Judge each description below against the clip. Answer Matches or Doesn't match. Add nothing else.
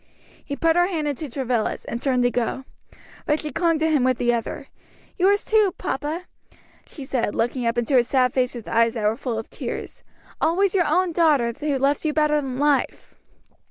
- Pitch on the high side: Matches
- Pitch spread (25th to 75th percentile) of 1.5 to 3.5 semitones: Doesn't match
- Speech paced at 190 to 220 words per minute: Matches